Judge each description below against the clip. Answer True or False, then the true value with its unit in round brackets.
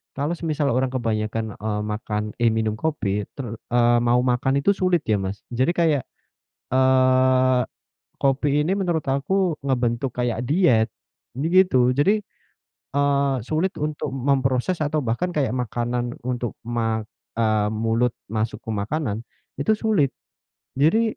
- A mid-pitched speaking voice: False (130 Hz)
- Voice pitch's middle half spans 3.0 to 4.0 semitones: False (4.4 semitones)